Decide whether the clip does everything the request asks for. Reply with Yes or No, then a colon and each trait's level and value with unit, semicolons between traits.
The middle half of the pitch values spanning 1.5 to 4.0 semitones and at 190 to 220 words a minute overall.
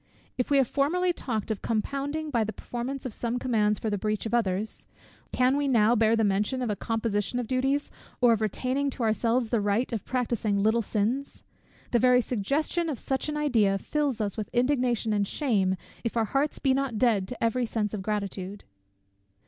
Yes: average, 3.7 semitones; average, 195 wpm